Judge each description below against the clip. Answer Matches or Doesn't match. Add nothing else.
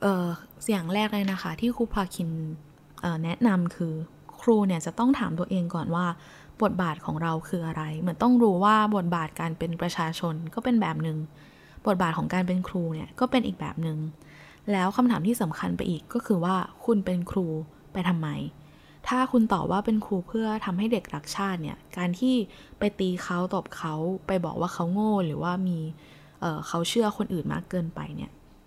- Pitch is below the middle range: Doesn't match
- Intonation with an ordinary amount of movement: Matches